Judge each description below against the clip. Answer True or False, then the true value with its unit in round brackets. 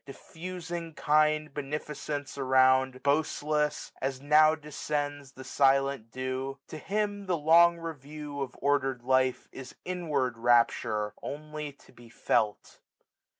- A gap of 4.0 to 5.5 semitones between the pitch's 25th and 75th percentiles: False (2.7 semitones)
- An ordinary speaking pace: False (120 wpm)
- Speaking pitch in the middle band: True (145 Hz)